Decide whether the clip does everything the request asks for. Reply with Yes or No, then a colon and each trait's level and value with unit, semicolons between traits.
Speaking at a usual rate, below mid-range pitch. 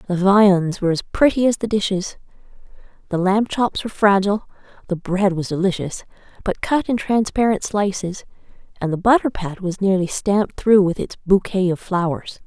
No: average, 170 wpm; high, 195 Hz